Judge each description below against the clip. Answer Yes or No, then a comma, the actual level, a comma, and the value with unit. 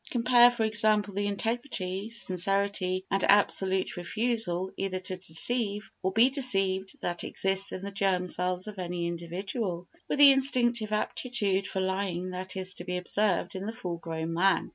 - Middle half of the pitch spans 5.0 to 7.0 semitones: No, average, 2.9 semitones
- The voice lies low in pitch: No, high, 195 Hz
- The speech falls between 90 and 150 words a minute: No, average, 165 wpm